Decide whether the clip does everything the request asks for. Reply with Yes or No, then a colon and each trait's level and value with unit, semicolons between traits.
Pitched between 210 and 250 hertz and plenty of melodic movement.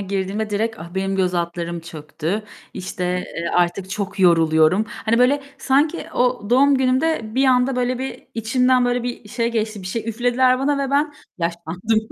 Yes: high, 220 Hz; wide, 5.7 semitones